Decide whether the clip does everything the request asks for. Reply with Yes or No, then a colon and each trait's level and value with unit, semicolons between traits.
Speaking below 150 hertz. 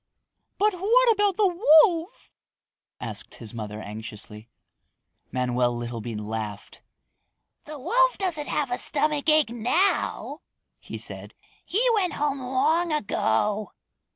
No: very high, 285 Hz